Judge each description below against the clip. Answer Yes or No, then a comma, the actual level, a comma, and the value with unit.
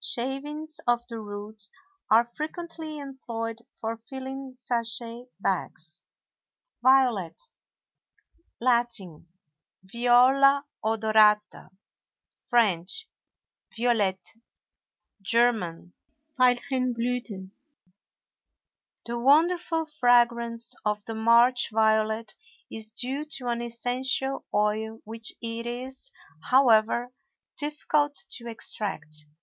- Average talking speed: No, slow, 75 wpm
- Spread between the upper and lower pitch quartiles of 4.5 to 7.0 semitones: No, average, 3.2 semitones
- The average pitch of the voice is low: No, high, 235 Hz